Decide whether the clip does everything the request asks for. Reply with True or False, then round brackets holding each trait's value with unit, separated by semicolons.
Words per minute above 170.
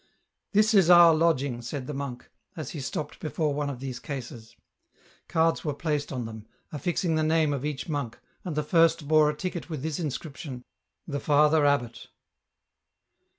True (180 wpm)